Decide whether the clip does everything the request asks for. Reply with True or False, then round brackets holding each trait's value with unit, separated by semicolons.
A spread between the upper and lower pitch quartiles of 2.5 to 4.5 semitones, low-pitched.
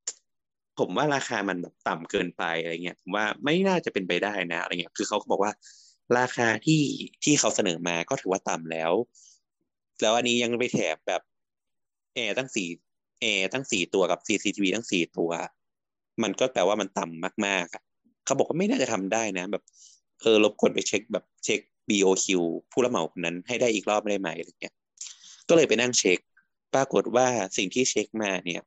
False (5.2 semitones; 100 Hz)